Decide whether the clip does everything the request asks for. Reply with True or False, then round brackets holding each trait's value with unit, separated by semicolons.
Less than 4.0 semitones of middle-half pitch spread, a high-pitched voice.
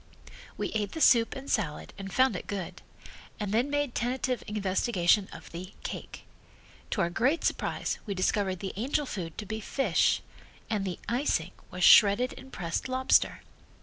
False (5.2 semitones; 210 Hz)